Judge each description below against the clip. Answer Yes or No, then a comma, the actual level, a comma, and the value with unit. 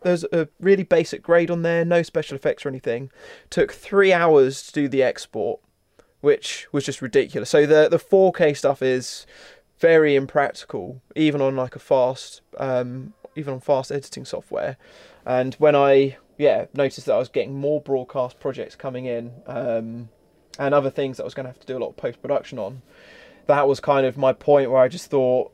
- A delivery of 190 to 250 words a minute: Yes, average, 195 wpm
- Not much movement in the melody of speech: No, average, 3.2 semitones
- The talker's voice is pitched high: No, medium, 140 Hz